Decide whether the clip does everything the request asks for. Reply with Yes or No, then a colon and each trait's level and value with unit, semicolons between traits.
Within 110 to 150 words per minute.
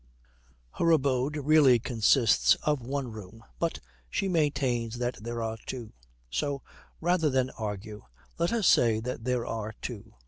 Yes: average, 145 wpm